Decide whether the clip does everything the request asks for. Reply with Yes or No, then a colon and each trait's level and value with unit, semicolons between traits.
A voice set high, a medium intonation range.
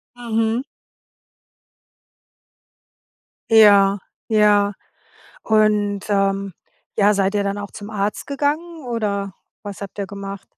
No: high, 205 Hz; narrow, 1.9 semitones